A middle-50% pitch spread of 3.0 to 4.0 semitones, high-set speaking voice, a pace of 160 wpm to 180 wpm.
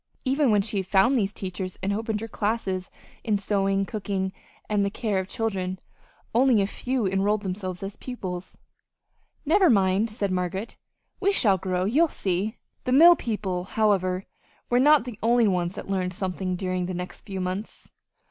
Yes: average, 3.3 semitones; high, 200 Hz; average, 170 wpm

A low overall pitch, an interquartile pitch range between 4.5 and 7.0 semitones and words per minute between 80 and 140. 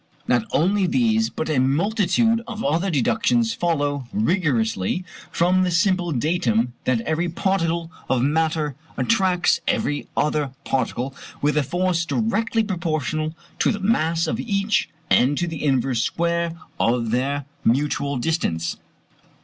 No: medium, 165 Hz; average, 5.2 semitones; slow, 135 wpm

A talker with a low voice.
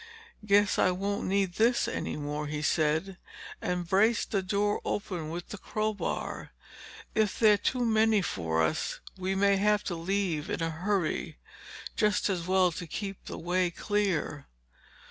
No: high, 190 Hz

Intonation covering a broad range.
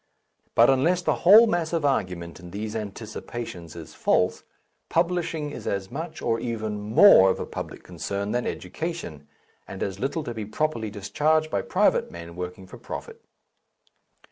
Yes: wide, 8.4 semitones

